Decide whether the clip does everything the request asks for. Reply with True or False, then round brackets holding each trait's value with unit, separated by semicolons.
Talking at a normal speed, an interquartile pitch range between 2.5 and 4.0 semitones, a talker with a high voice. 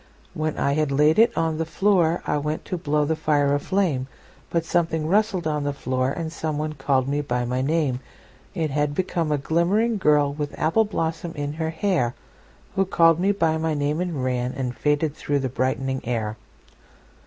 False (165 wpm; 3.0 semitones; 150 Hz)